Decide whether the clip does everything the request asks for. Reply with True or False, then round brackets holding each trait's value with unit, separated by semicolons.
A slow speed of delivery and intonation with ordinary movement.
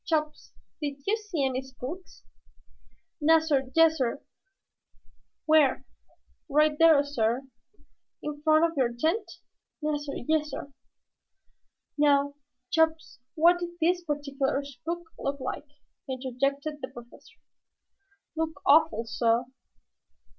True (100 wpm; 3.1 semitones)